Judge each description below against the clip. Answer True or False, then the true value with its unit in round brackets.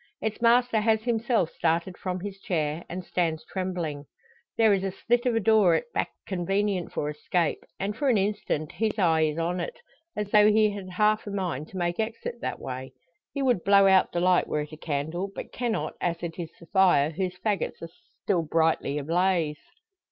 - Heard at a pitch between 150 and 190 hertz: True (185 Hz)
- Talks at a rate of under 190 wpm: False (200 wpm)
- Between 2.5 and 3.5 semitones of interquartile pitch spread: False (4.2 semitones)